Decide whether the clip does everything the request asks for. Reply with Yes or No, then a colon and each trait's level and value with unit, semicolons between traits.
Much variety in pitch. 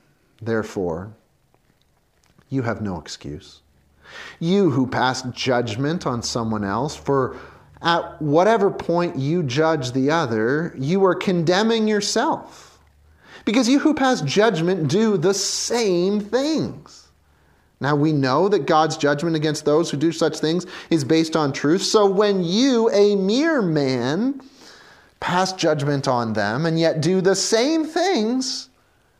Yes: wide, 7.8 semitones